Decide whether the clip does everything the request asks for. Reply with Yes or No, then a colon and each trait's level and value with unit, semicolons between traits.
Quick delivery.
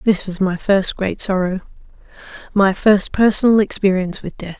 No: average, 145 wpm